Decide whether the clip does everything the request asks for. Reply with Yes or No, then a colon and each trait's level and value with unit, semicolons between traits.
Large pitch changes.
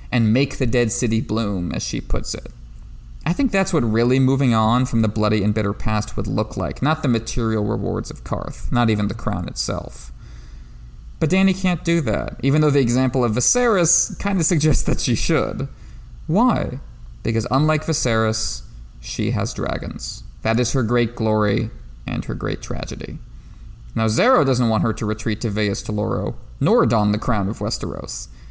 No: average, 3.9 semitones